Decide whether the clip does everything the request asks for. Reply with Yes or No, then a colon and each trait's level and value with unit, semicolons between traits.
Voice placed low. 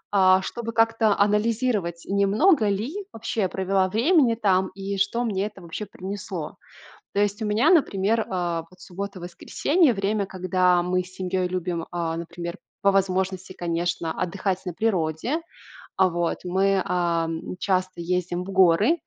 No: high, 190 Hz